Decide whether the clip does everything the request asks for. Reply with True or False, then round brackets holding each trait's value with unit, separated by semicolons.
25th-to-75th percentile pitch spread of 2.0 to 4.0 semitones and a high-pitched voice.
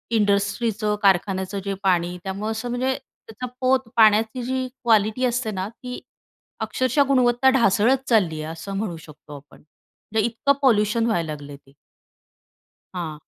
False (4.4 semitones; 215 Hz)